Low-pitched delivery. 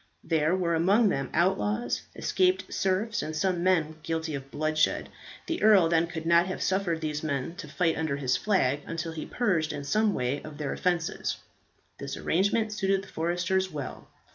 No: medium, 170 Hz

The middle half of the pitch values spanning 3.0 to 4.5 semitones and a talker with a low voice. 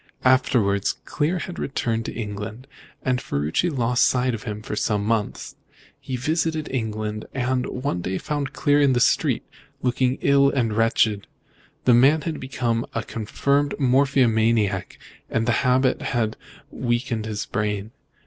Yes: average, 3.8 semitones; low, 120 Hz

